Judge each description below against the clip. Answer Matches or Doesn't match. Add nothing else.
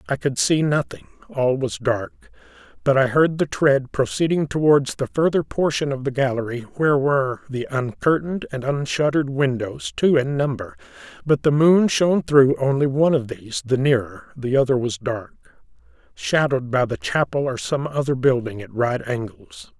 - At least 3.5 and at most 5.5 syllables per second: Matches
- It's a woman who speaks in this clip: Doesn't match